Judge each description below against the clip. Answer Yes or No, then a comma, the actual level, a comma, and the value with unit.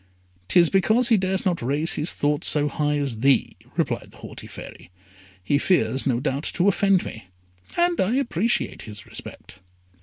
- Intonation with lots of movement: Yes, wide, 6.1 semitones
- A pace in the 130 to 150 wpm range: No, average, 170 wpm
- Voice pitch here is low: No, medium, 155 Hz